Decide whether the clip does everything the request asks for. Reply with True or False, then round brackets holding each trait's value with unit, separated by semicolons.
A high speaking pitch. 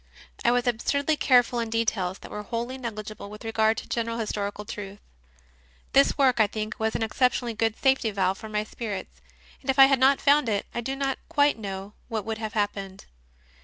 True (225 Hz)